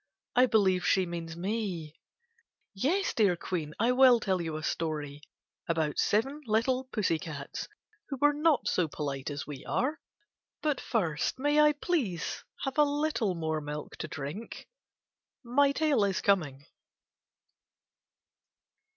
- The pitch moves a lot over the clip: Yes, wide, 8.9 semitones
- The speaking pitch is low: No, high, 195 Hz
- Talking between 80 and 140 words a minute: Yes, slow, 135 wpm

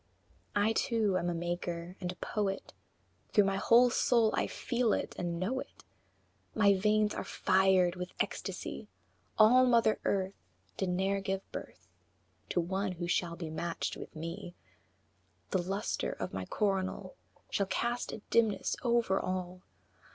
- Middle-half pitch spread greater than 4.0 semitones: No, average, 3.3 semitones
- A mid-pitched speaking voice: No, high, 195 Hz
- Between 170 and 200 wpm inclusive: No, average, 150 wpm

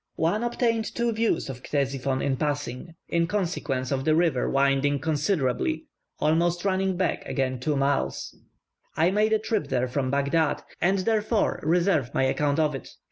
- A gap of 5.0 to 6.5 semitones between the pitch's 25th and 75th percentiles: Yes, wide, 5.5 semitones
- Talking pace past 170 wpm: No, average, 160 wpm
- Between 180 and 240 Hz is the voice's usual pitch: No, medium, 155 Hz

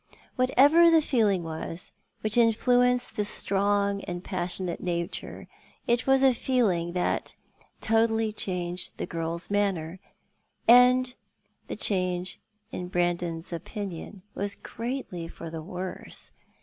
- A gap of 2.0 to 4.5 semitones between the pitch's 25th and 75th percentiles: No, average, 5.2 semitones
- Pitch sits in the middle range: No, high, 200 Hz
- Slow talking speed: Yes, slow, 125 wpm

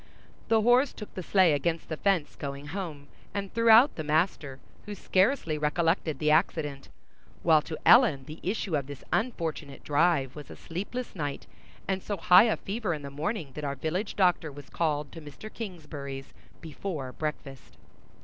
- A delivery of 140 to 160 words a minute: No, average, 170 wpm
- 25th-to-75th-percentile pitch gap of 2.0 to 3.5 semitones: No, average, 5.1 semitones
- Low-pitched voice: No, medium, 160 Hz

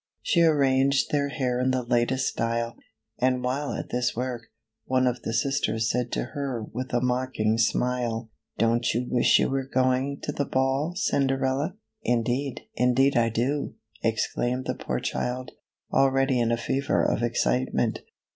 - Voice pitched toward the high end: No, low, 125 Hz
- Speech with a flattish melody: Yes, narrow, 2.2 semitones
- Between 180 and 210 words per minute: No, average, 165 wpm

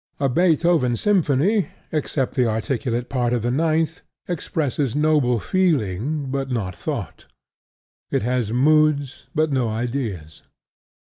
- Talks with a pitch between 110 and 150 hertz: Yes, low, 135 Hz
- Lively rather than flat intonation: No, average, 4.4 semitones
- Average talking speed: No, slow, 120 wpm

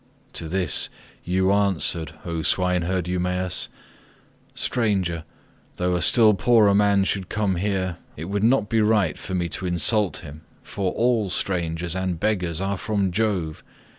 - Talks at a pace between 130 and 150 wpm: Yes, average, 145 wpm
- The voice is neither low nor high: No, very low, 95 Hz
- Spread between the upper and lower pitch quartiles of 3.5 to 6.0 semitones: No, average, 2.7 semitones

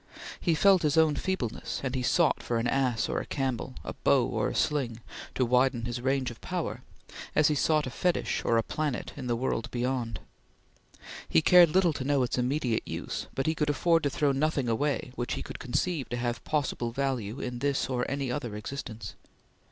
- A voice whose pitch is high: No, low, 130 Hz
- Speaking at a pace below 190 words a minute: No, average, 200 wpm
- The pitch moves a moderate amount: Yes, average, 3.5 semitones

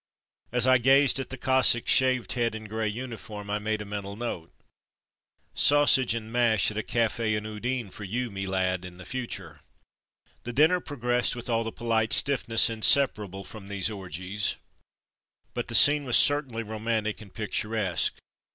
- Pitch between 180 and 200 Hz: No, low, 110 Hz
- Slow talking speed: No, average, 175 wpm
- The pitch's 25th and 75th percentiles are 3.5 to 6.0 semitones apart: No, average, 3.1 semitones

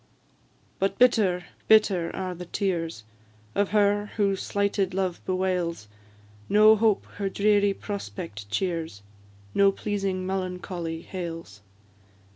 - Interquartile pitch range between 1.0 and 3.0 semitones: Yes, average, 2.7 semitones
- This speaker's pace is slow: Yes, slow, 105 wpm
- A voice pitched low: No, high, 190 Hz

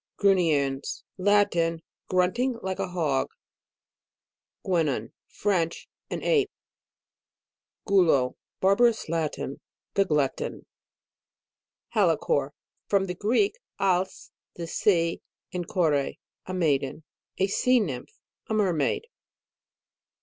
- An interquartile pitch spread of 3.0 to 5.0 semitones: Yes, average, 4.4 semitones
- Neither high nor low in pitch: Yes, medium, 180 Hz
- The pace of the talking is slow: Yes, slow, 90 wpm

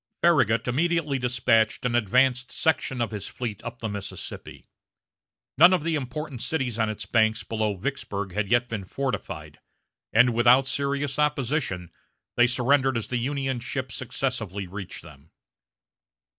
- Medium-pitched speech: No, low, 125 Hz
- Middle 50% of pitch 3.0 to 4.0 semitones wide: Yes, average, 3.7 semitones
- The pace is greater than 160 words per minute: No, average, 145 wpm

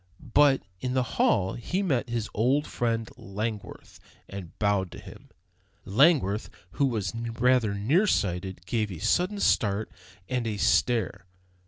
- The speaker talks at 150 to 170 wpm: No, average, 140 wpm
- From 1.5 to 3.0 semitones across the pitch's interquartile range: No, average, 4.2 semitones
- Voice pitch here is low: Yes, low, 115 Hz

